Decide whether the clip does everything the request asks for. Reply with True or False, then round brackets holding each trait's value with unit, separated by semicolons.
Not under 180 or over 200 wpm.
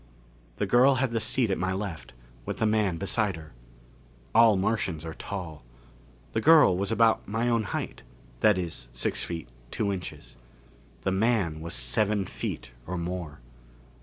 False (160 wpm)